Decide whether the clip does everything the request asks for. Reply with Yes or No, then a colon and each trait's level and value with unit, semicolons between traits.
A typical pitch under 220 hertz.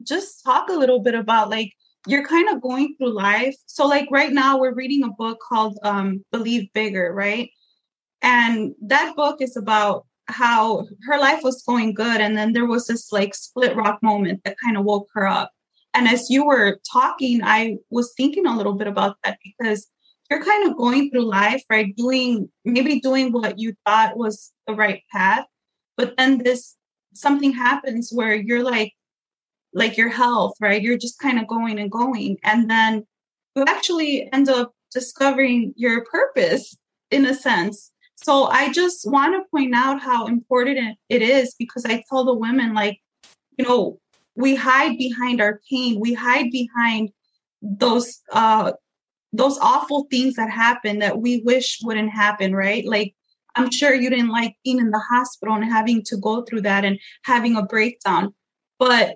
No: high, 240 Hz